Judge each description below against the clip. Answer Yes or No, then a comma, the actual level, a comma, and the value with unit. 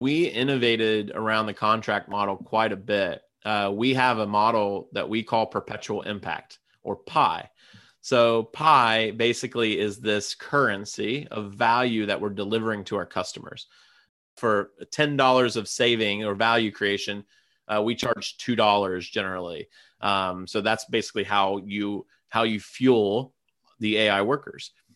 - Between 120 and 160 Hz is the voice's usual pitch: No, low, 110 Hz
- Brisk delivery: No, average, 140 wpm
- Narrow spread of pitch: Yes, narrow, 2.1 semitones